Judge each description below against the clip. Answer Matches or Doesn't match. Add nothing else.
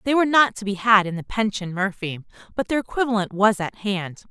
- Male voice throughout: Doesn't match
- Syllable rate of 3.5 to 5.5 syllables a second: Doesn't match